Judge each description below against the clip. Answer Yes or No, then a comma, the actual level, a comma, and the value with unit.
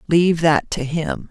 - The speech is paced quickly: No, average, 185 wpm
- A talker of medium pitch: Yes, medium, 160 Hz